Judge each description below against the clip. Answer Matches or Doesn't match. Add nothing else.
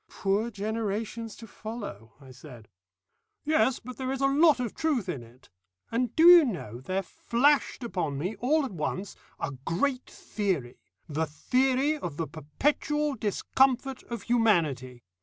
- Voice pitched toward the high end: Matches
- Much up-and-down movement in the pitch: Matches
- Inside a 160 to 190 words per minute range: Doesn't match